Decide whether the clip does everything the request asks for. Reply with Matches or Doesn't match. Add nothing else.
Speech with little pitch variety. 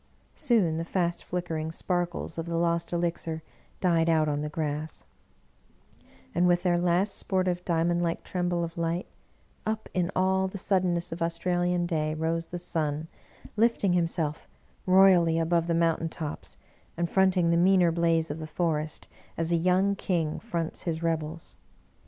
Matches